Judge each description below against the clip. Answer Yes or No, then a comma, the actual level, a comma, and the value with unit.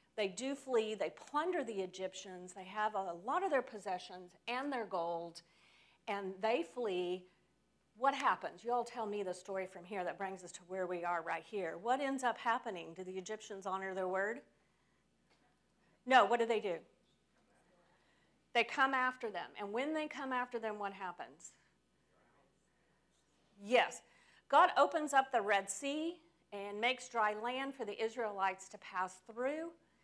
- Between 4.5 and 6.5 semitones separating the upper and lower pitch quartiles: Yes, average, 5.1 semitones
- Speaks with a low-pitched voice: No, high, 210 Hz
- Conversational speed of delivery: Yes, average, 165 wpm